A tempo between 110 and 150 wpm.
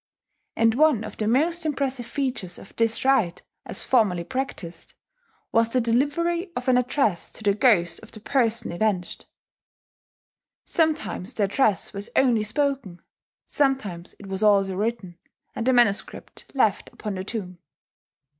Yes: average, 145 wpm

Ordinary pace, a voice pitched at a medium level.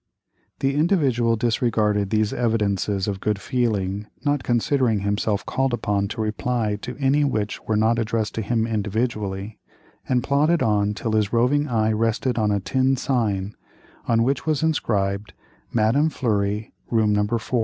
No: average, 155 wpm; low, 110 Hz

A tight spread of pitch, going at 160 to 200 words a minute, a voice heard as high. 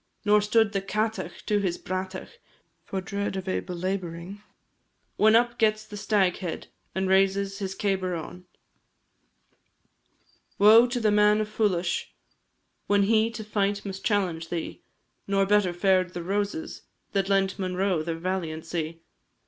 No: narrow, 2.3 semitones; average, 140 wpm; high, 195 Hz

